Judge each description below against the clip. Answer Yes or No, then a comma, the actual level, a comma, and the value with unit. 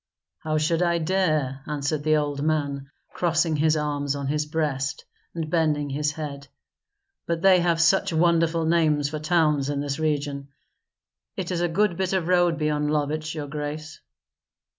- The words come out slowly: No, average, 160 wpm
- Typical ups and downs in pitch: No, narrow, 2.3 semitones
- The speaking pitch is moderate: Yes, medium, 155 Hz